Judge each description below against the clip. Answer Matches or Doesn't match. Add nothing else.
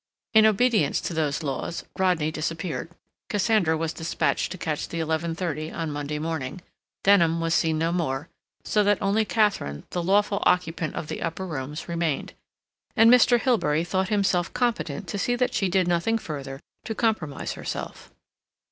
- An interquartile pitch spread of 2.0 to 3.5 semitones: Doesn't match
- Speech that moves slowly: Doesn't match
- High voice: Doesn't match